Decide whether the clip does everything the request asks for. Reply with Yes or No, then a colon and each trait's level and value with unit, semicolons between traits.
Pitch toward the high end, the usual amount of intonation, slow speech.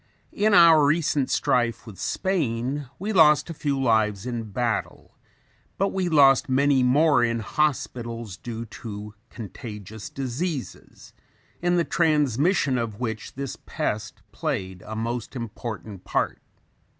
No: low, 125 Hz; average, 5.0 semitones; slow, 125 wpm